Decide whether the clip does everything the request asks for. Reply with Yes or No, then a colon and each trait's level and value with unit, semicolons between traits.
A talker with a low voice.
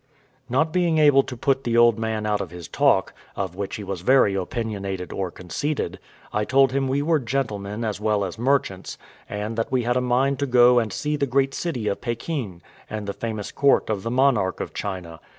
Yes: low, 115 Hz